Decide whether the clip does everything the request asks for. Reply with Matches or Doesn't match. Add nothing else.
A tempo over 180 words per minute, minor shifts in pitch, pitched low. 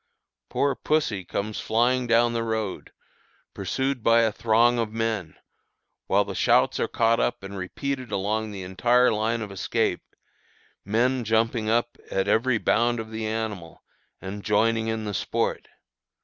Doesn't match